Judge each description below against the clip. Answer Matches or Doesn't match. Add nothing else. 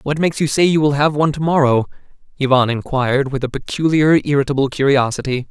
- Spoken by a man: Matches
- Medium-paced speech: Matches